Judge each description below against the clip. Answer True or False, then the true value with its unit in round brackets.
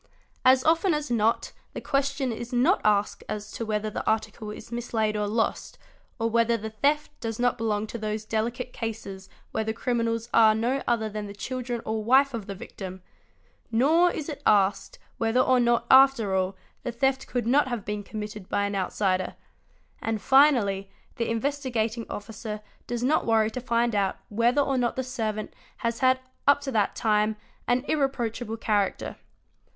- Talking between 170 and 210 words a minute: True (175 wpm)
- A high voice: True (230 Hz)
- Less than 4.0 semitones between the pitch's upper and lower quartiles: True (3.1 semitones)